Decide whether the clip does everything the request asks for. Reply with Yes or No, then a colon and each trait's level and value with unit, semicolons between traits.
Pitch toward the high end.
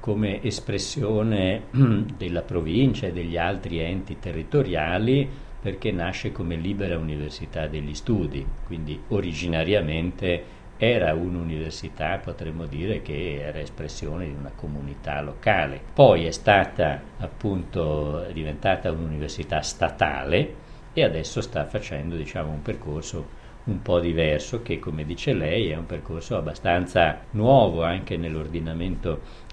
No: very low, 85 Hz